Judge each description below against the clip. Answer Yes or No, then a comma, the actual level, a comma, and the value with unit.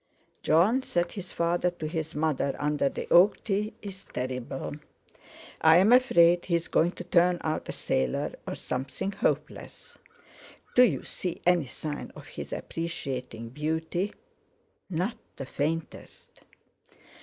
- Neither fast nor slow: No, slow, 130 wpm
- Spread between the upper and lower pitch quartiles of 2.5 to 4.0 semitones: Yes, average, 3.5 semitones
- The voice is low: No, medium, 165 Hz